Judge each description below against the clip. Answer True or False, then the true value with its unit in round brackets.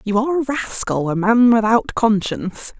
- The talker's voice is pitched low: False (225 Hz)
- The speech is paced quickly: False (170 wpm)